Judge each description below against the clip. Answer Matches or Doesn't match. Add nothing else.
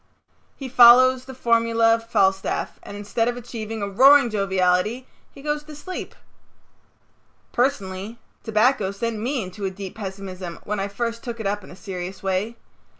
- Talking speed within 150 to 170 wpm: Matches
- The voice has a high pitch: Matches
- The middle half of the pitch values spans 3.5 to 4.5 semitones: Matches